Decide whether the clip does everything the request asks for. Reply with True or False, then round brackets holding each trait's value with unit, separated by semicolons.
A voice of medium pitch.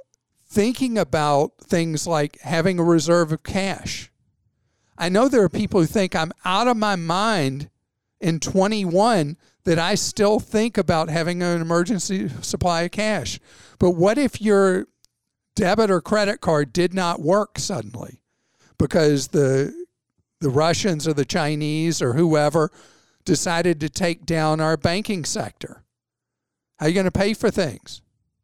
True (170 Hz)